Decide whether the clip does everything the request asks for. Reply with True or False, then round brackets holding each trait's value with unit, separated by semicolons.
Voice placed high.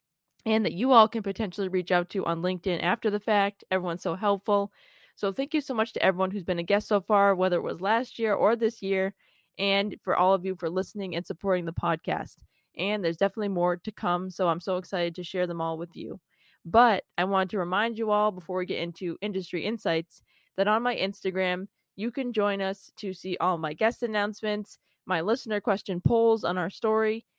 True (195 Hz)